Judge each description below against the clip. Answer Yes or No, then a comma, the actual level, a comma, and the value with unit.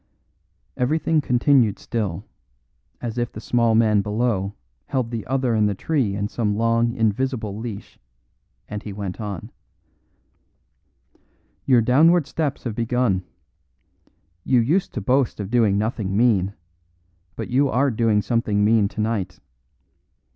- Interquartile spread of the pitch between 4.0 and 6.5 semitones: No, average, 3.3 semitones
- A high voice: No, low, 115 Hz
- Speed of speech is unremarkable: No, slow, 130 wpm